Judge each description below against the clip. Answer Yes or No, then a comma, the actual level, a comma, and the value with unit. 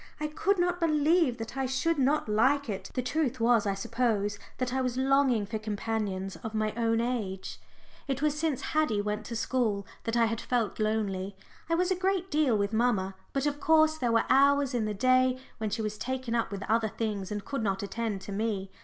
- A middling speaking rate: No, fast, 215 wpm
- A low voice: No, high, 235 Hz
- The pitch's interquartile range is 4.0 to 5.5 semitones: Yes, average, 4.7 semitones